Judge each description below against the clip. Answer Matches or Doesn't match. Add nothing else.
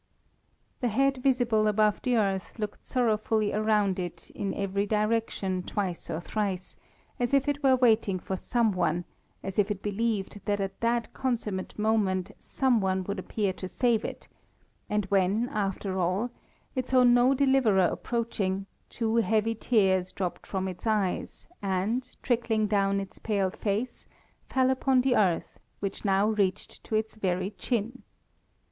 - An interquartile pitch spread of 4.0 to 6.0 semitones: Doesn't match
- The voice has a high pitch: Matches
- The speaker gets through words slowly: Doesn't match